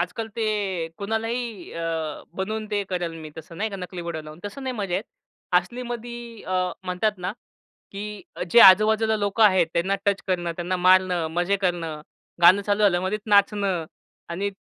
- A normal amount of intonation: Yes, average, 3.4 semitones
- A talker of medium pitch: No, high, 195 Hz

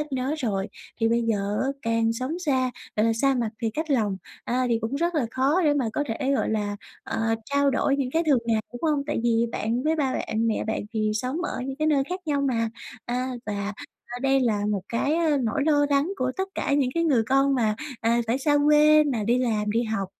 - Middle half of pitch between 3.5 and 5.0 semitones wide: Yes, average, 4.3 semitones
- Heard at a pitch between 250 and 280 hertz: Yes, very high, 255 Hz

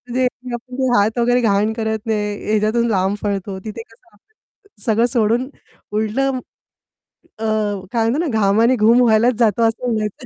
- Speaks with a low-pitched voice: No, high, 225 Hz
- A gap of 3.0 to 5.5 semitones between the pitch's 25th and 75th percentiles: No, narrow, 2.5 semitones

